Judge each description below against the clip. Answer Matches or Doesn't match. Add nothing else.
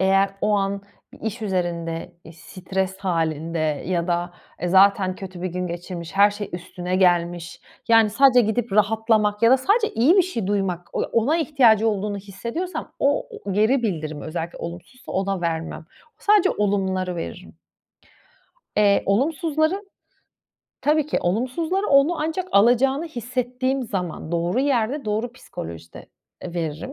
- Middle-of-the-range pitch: Doesn't match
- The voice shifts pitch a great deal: Matches